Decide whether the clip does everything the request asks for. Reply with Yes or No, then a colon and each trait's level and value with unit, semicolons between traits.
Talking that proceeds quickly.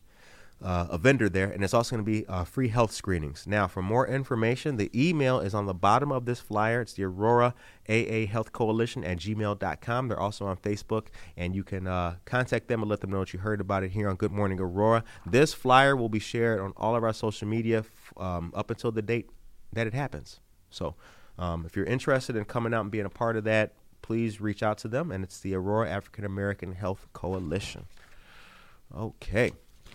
Yes: fast, 215 wpm